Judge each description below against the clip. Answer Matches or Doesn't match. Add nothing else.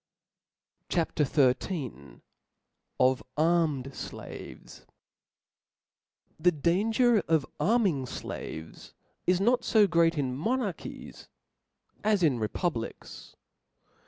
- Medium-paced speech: Doesn't match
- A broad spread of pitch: Matches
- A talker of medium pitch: Matches